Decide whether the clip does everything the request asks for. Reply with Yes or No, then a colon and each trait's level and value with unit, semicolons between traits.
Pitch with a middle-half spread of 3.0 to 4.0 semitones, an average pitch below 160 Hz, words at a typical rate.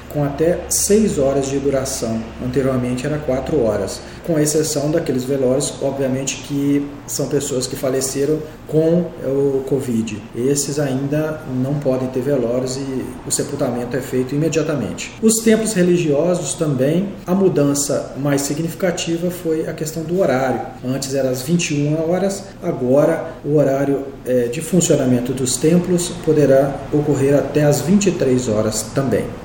Yes: average, 3.4 semitones; medium, 140 Hz; average, 135 wpm